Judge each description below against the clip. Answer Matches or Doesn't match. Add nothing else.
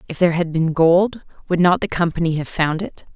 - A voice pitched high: Doesn't match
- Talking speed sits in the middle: Doesn't match